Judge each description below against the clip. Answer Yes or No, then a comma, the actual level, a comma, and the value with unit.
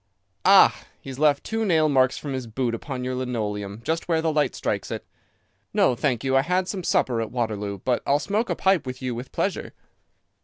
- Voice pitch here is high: No, low, 130 Hz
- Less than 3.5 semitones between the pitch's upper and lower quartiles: No, average, 4.7 semitones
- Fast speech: Yes, fast, 215 wpm